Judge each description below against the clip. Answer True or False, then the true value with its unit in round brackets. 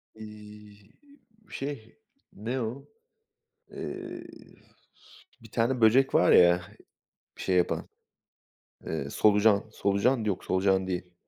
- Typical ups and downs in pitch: True (3.2 semitones)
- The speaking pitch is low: True (105 Hz)